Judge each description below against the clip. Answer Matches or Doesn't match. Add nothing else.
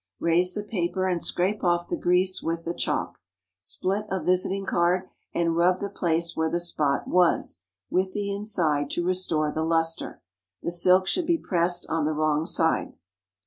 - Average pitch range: Doesn't match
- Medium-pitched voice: Matches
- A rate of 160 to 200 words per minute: Matches